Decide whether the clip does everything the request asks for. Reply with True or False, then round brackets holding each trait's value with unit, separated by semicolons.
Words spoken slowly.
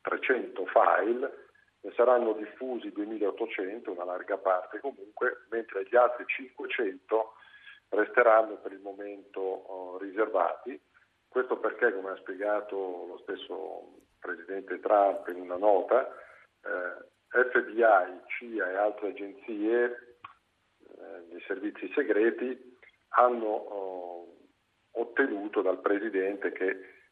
True (105 wpm)